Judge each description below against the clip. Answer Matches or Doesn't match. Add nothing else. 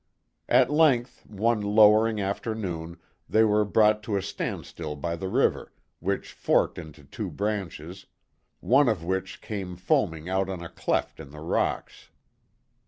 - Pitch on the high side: Doesn't match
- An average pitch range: Matches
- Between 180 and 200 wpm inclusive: Doesn't match